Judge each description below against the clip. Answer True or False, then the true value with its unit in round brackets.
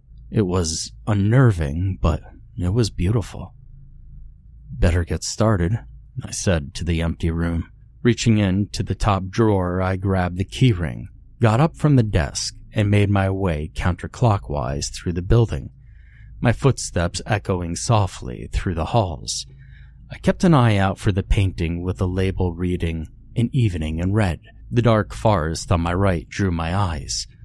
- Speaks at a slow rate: False (155 wpm)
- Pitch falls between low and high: False (100 Hz)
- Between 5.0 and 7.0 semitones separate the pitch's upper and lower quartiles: False (4.6 semitones)